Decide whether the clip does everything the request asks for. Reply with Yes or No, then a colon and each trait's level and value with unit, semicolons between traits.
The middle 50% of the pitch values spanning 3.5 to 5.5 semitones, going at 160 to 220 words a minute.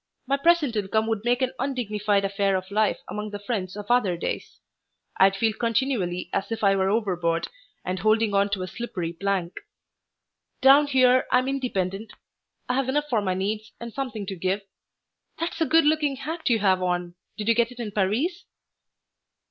Yes: average, 4.5 semitones; average, 180 wpm